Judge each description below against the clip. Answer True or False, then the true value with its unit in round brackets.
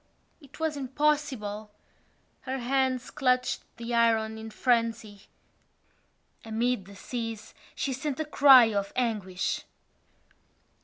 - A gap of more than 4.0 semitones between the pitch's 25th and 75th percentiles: False (3.2 semitones)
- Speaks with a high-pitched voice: True (240 Hz)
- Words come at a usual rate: False (105 wpm)